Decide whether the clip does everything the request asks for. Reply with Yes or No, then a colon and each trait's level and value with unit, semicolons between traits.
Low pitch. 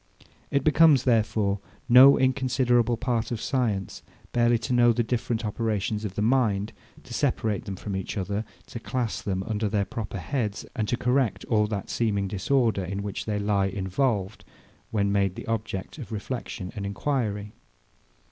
Yes: low, 110 Hz